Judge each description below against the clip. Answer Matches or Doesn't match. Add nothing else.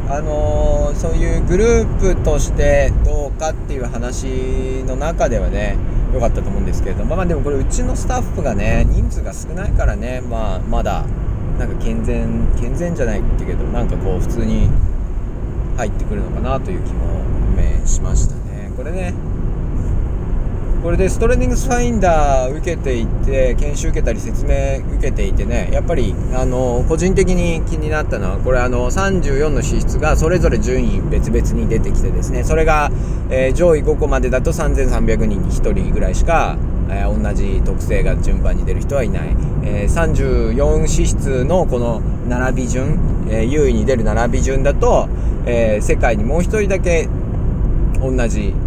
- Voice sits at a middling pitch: Doesn't match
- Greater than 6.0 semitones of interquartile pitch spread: Doesn't match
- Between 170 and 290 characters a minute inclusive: Doesn't match